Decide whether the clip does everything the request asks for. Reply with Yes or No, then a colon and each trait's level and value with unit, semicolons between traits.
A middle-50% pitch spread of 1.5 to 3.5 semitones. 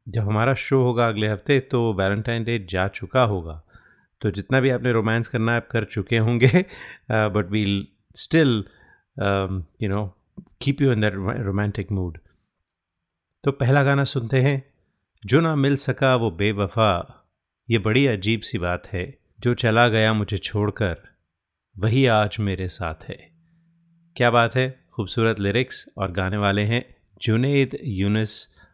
No: average, 4.4 semitones